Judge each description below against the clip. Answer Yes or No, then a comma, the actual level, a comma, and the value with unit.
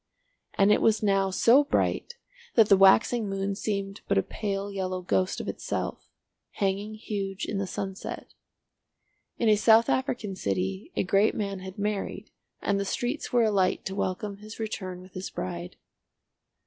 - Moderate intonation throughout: No, narrow, 2.1 semitones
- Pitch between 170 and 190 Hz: No, high, 200 Hz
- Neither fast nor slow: Yes, average, 160 wpm